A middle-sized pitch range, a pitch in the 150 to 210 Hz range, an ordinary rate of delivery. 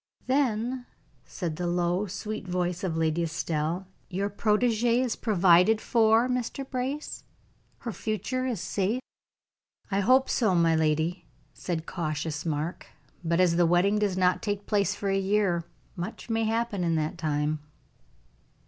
Yes: average, 4.6 semitones; high, 190 Hz; average, 145 wpm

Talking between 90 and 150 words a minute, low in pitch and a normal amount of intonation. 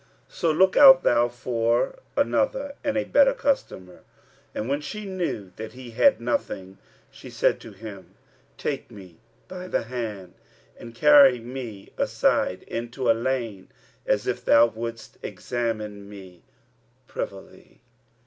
No: average, 140 wpm; low, 120 Hz; wide, 5.9 semitones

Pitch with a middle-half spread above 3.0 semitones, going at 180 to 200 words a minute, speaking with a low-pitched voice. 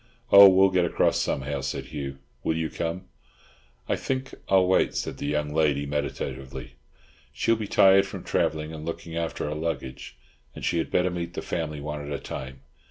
Yes: average, 4.1 semitones; average, 185 wpm; very low, 80 Hz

